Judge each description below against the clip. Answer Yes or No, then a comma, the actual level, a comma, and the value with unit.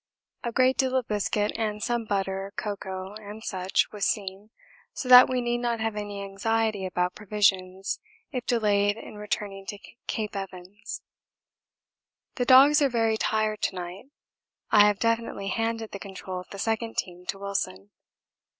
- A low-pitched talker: No, high, 210 Hz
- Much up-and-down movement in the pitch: No, average, 2.7 semitones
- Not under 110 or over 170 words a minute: Yes, average, 155 wpm